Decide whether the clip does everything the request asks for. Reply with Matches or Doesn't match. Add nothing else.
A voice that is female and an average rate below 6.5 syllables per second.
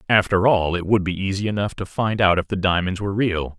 Doesn't match